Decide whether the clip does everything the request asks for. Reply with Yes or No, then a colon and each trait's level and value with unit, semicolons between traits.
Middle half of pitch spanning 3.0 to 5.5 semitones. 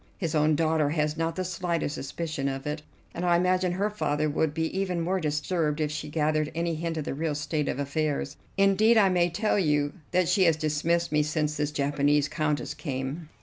No: narrow, 2.6 semitones